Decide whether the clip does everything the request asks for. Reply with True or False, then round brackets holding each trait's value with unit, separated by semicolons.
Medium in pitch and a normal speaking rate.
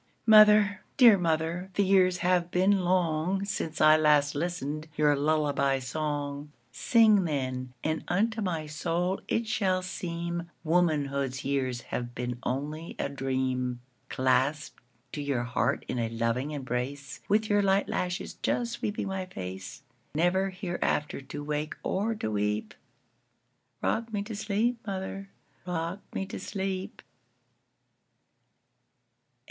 False (160 Hz; 110 wpm)